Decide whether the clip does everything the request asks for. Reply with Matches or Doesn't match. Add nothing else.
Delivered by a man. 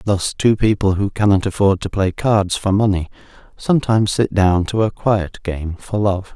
Matches